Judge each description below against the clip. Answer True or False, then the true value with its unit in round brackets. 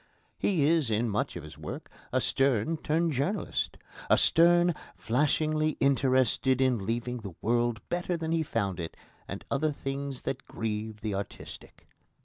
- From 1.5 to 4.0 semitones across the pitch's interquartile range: False (5.6 semitones)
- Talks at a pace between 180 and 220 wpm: False (150 wpm)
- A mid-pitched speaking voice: False (130 Hz)